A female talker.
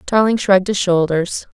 Yes: female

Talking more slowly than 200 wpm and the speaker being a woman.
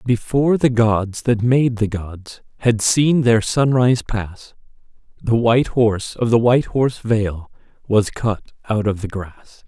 No: average, 160 wpm; male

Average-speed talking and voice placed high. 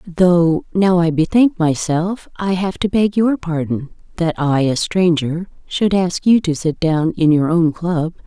No: average, 175 wpm; medium, 170 Hz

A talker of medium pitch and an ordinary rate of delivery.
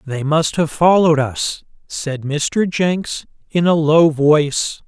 Yes: medium, 155 Hz; average, 150 wpm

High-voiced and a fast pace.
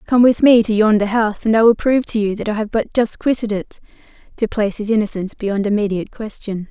Yes: high, 215 Hz; fast, 225 wpm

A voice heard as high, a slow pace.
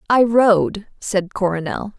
Yes: high, 200 Hz; slow, 120 wpm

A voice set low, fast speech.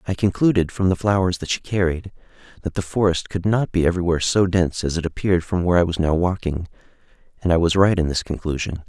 Yes: very low, 90 Hz; fast, 225 wpm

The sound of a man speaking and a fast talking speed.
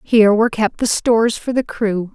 No: female; fast, 225 wpm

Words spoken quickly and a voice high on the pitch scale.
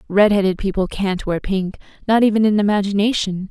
No: average, 155 wpm; high, 200 Hz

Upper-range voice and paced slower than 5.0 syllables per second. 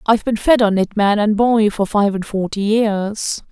Yes: high, 210 Hz; 4.5 syllables/s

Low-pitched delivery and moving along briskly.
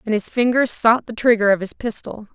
No: high, 225 Hz; fast, 230 wpm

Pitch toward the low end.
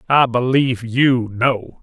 Yes: low, 125 Hz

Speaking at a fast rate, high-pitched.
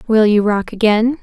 No: average, 195 wpm; high, 220 Hz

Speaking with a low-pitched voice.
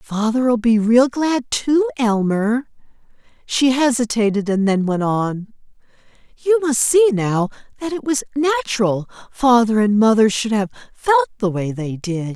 No: high, 235 Hz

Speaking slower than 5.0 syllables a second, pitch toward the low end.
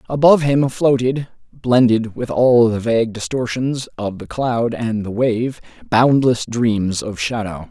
Yes: 4.0 syllables/s; low, 120 Hz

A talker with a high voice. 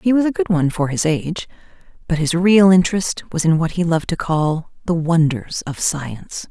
No: medium, 170 Hz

